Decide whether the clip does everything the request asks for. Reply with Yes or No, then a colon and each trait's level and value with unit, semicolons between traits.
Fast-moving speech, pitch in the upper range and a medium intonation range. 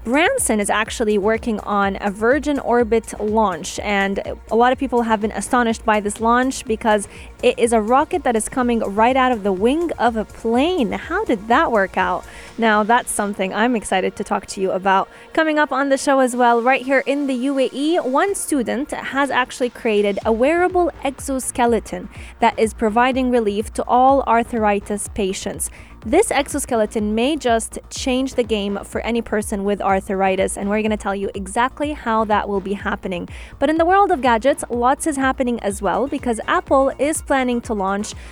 No: average, 185 wpm; high, 235 Hz; average, 4.1 semitones